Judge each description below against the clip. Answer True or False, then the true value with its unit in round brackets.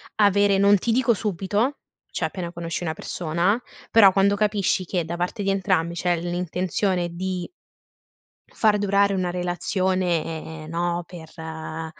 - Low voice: False (180 Hz)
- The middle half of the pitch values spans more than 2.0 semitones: True (2.7 semitones)